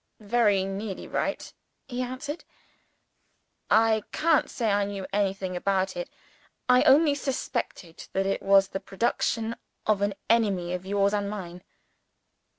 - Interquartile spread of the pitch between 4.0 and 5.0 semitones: No, average, 3.3 semitones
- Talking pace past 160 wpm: No, slow, 135 wpm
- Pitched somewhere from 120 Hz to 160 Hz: No, high, 200 Hz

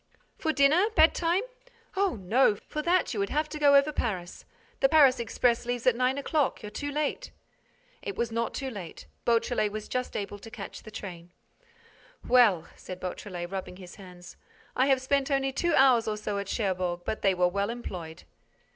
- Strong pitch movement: Yes, wide, 6.0 semitones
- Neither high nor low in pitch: No, high, 235 Hz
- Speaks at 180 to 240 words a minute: Yes, average, 185 wpm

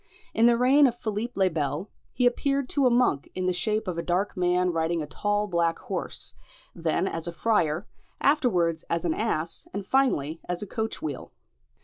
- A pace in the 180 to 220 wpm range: Yes, average, 195 wpm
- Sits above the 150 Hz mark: Yes, medium, 185 Hz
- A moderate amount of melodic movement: No, wide, 5.7 semitones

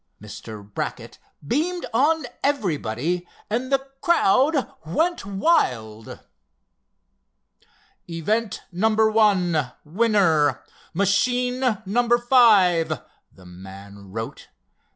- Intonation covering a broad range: Yes, wide, 8.8 semitones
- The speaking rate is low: Yes, slow, 75 wpm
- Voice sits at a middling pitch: No, high, 200 Hz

